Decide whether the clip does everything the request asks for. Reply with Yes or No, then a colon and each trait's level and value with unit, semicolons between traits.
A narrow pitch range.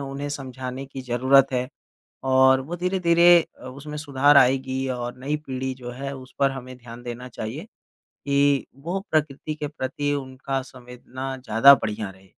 Yes: narrow, 1.9 semitones